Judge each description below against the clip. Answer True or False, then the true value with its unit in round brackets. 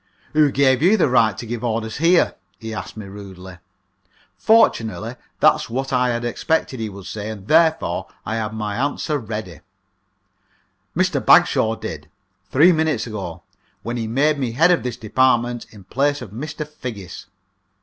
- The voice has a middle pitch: False (120 Hz)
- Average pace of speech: True (165 wpm)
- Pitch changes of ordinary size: True (4.9 semitones)